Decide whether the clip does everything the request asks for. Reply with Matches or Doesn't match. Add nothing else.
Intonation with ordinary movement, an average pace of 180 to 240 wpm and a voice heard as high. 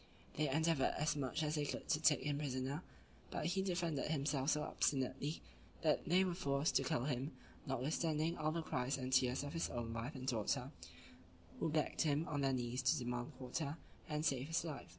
Doesn't match